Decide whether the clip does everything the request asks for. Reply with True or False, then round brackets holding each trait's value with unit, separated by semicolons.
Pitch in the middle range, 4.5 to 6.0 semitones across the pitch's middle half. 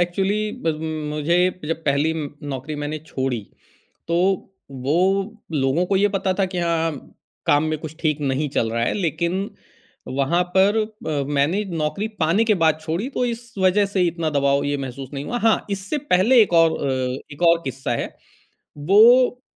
True (160 Hz; 5.2 semitones)